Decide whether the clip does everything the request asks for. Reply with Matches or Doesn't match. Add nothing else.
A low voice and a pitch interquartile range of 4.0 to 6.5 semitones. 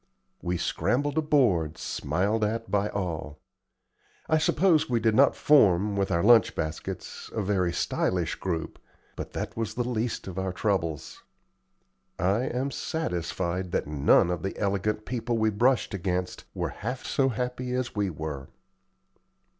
Matches